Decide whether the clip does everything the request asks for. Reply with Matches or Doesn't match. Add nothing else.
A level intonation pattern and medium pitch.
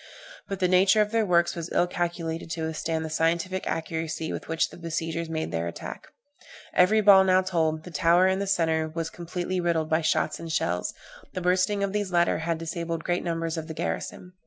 Matches